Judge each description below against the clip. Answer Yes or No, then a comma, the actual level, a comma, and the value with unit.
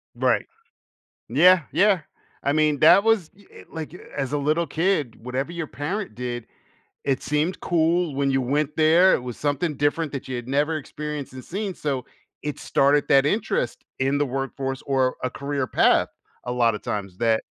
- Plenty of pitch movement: No, average, 3.5 semitones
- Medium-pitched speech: Yes, medium, 145 Hz